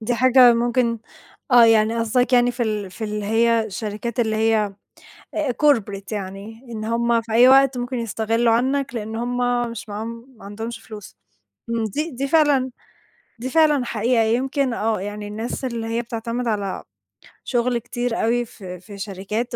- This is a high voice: Yes, high, 230 Hz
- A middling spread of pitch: No, narrow, 2.2 semitones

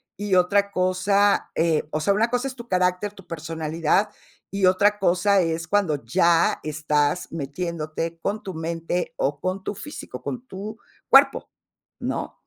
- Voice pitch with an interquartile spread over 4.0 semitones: No, average, 3.7 semitones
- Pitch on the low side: No, medium, 180 Hz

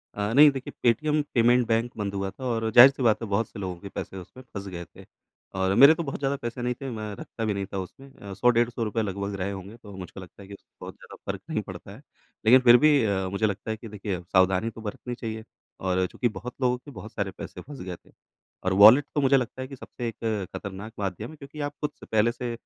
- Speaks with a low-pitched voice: Yes, low, 110 Hz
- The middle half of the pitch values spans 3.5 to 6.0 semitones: Yes, average, 3.9 semitones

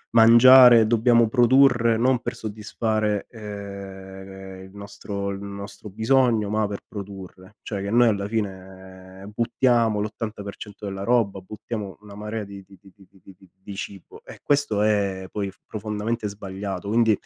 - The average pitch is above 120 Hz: No, low, 105 Hz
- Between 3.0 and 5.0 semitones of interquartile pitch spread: No, narrow, 2.4 semitones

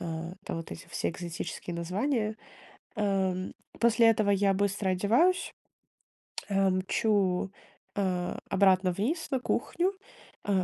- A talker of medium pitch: No, high, 195 Hz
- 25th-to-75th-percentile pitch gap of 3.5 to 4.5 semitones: No, average, 2.9 semitones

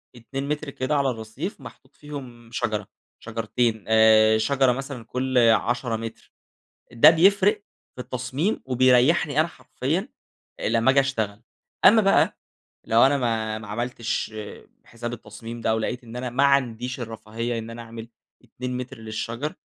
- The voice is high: No, low, 120 Hz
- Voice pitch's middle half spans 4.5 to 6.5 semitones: No, average, 3.3 semitones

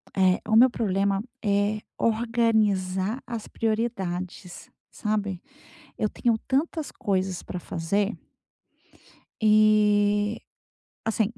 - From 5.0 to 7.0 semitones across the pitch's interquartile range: No, narrow, 2.6 semitones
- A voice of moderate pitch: No, high, 210 Hz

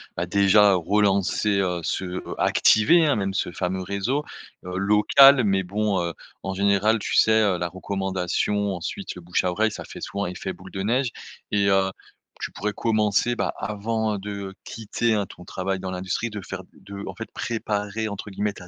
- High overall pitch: No, low, 100 Hz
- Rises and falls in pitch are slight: Yes, narrow, 2.2 semitones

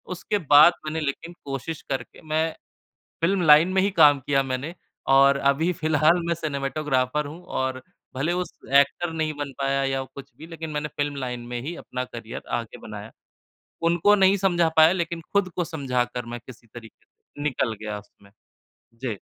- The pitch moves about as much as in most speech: Yes, average, 4.2 semitones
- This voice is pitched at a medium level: Yes, medium, 145 Hz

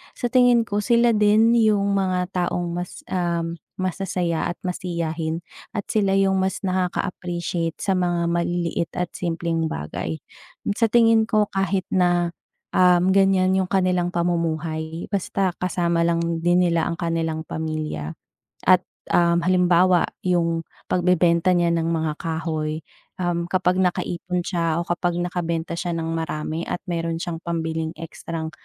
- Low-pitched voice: No, medium, 175 Hz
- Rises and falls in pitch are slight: Yes, narrow, 1.9 semitones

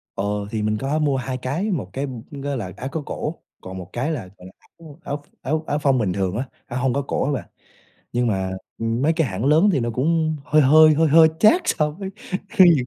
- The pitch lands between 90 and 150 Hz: Yes, medium, 140 Hz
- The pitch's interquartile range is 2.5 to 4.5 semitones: No, average, 4.9 semitones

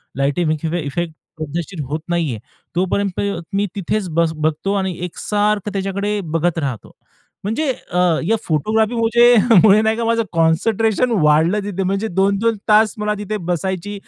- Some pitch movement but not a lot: Yes, average, 4.3 semitones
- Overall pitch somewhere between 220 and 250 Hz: No, high, 195 Hz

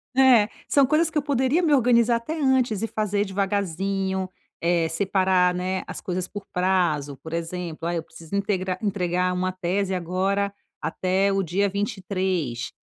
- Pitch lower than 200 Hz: Yes, high, 190 Hz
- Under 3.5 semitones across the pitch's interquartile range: Yes, narrow, 2.5 semitones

